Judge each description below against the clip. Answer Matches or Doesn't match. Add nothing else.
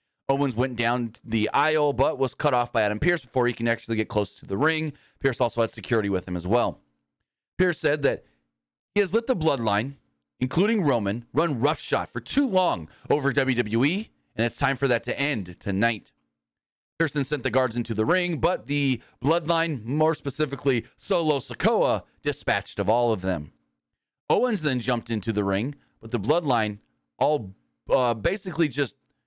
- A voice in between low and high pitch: Doesn't match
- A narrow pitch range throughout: Doesn't match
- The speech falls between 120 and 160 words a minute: Doesn't match